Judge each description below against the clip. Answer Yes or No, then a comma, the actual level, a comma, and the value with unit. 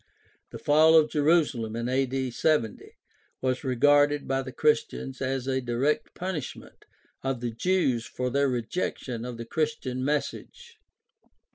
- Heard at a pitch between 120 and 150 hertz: Yes, low, 135 Hz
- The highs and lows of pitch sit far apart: No, average, 3.4 semitones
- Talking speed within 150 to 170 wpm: No, average, 140 wpm